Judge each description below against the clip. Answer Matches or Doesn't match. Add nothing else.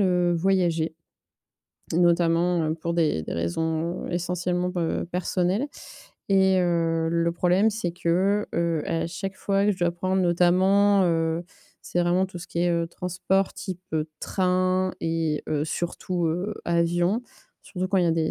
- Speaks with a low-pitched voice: Doesn't match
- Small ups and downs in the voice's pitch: Matches